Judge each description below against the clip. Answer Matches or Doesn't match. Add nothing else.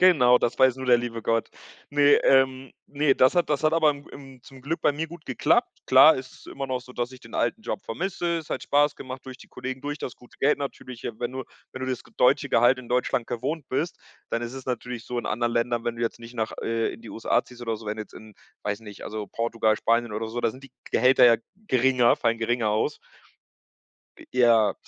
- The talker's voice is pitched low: Matches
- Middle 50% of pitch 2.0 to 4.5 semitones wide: Matches